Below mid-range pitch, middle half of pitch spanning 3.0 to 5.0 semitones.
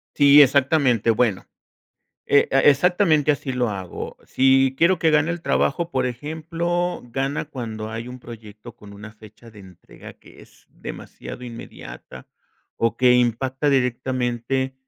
Yes: low, 130 Hz; average, 4.1 semitones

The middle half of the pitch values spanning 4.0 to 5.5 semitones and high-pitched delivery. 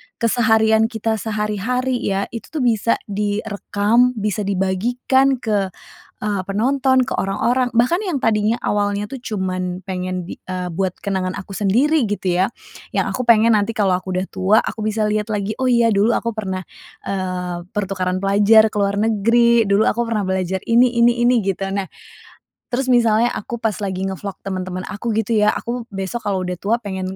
No: average, 3.4 semitones; high, 210 Hz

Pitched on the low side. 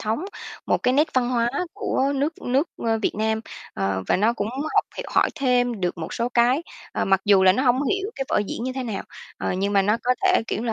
No: high, 240 Hz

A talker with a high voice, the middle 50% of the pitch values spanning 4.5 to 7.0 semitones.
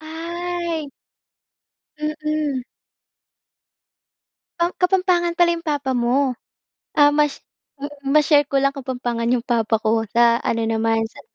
Yes: very high, 285 Hz; average, 5.0 semitones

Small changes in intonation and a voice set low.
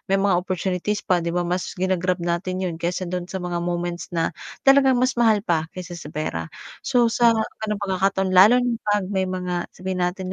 No: narrow, 2.2 semitones; medium, 185 Hz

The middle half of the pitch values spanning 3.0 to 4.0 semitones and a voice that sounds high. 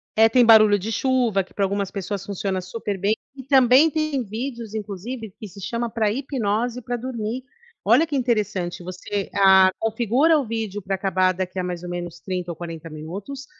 No: average, 4.4 semitones; high, 210 Hz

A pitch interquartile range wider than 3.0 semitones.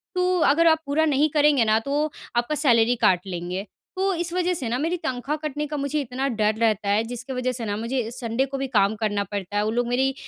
Yes: average, 5.2 semitones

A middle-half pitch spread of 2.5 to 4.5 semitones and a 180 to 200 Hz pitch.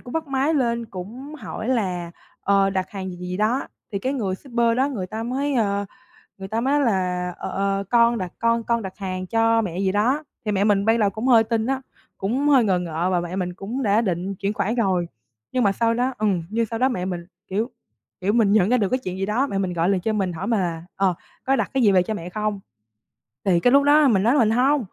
No: average, 4.1 semitones; high, 210 Hz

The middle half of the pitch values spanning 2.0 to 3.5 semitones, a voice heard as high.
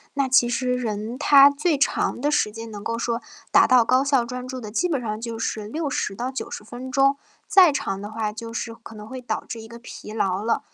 Yes: average, 3.1 semitones; high, 235 Hz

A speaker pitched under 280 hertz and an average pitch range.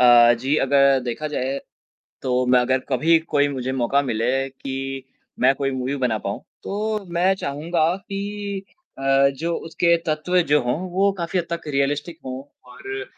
Yes: medium, 140 Hz; average, 4.5 semitones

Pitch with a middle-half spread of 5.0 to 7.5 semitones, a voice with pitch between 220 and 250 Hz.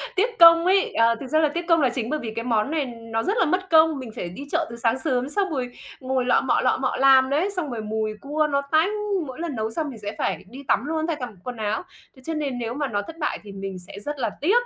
No: wide, 5.6 semitones; very high, 270 Hz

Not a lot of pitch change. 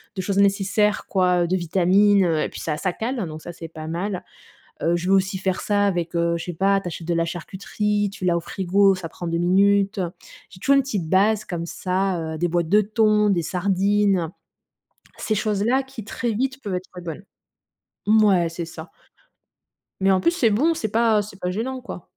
No: average, 3.2 semitones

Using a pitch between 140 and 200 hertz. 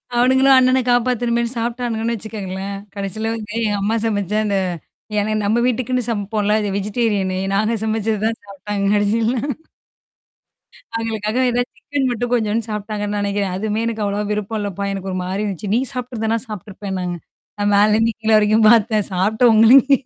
No: high, 215 Hz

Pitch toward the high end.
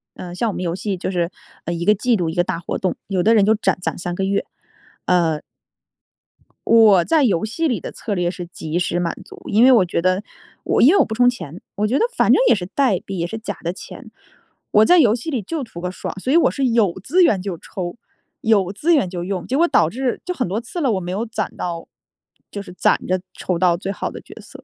Yes: high, 195 Hz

